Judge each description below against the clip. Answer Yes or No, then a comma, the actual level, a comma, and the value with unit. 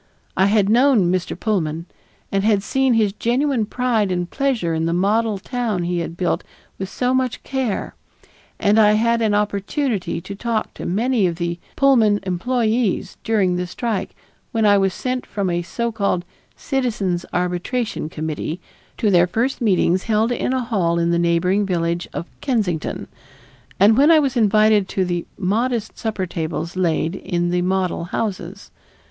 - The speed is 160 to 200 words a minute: Yes, average, 165 wpm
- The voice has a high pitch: Yes, high, 205 Hz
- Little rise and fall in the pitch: No, average, 4.6 semitones